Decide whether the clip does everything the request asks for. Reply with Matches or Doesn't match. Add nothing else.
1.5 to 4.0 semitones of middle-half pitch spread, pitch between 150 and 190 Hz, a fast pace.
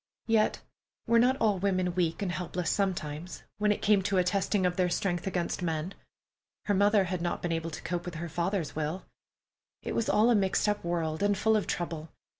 Matches